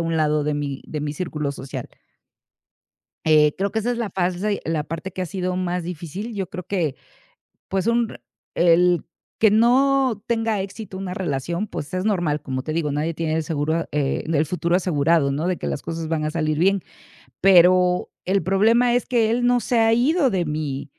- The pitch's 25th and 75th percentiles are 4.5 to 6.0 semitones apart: Yes, average, 5.0 semitones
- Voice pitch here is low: No, medium, 180 Hz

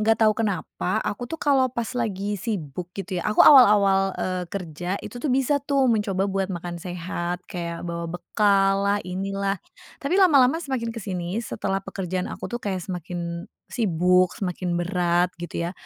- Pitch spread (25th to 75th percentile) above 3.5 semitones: Yes, average, 3.9 semitones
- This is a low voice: No, high, 195 Hz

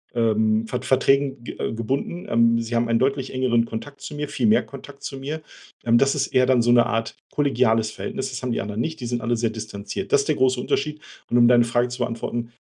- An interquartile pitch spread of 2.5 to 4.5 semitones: Yes, average, 2.9 semitones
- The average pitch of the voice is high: No, low, 120 Hz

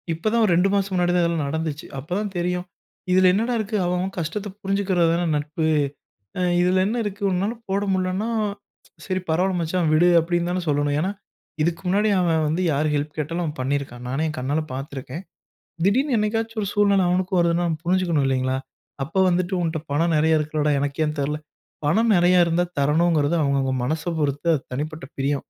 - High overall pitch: No, medium, 170 Hz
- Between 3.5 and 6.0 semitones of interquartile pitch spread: Yes, average, 3.9 semitones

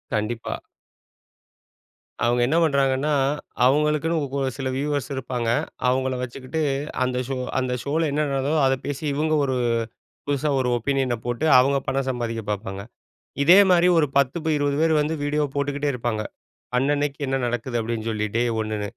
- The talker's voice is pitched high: No, low, 135 Hz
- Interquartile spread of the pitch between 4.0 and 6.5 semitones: No, average, 3.1 semitones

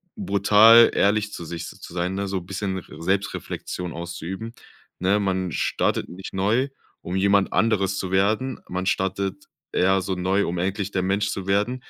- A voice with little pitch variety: Yes, narrow, 1.7 semitones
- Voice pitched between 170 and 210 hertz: No, very low, 95 Hz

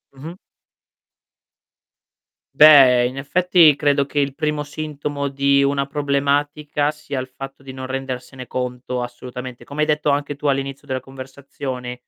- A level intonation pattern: Yes, narrow, 1.9 semitones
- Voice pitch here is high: No, medium, 140 Hz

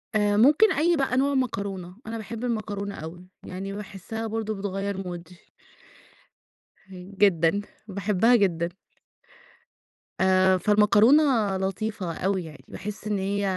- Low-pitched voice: No, high, 200 Hz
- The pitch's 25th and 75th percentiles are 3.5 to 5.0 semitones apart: No, average, 2.8 semitones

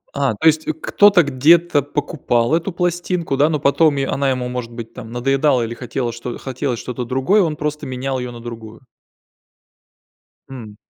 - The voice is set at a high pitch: No, low, 135 Hz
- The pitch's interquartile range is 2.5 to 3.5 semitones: No, average, 3.9 semitones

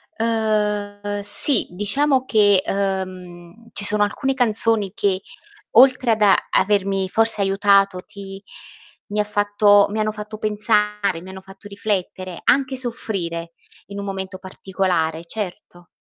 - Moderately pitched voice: No, high, 205 Hz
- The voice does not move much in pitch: Yes, narrow, 2.1 semitones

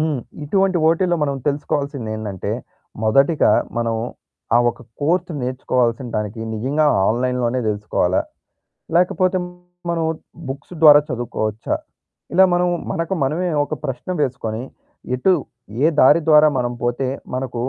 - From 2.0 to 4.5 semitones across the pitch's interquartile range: No, wide, 5.4 semitones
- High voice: No, low, 135 Hz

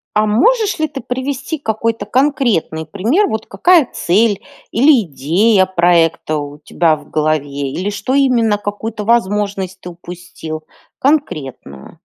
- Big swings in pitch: Yes, wide, 7.4 semitones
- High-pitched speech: Yes, high, 205 Hz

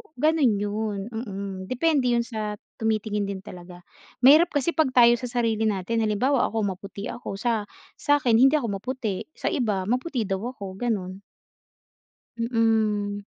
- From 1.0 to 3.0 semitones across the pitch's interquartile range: No, average, 3.6 semitones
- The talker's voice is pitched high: Yes, high, 220 Hz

